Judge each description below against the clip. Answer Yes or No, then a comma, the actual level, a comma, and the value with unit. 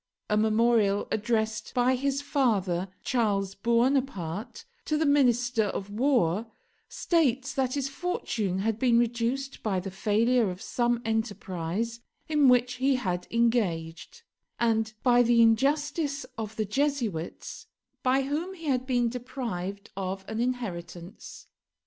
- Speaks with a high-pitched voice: Yes, high, 235 Hz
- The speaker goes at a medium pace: No, slow, 130 wpm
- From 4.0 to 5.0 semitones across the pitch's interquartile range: Yes, average, 4.3 semitones